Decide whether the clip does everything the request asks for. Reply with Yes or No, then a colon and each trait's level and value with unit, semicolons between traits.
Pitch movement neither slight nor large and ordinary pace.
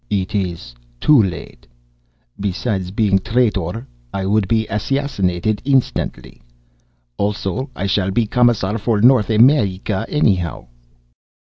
No: average, 3.5 semitones; slow, 115 wpm